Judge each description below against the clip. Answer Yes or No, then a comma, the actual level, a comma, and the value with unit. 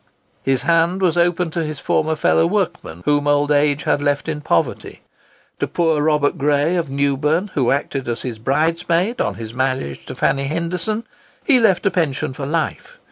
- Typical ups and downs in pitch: Yes, average, 3.5 semitones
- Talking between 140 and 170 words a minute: No, average, 180 wpm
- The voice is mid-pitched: Yes, medium, 150 Hz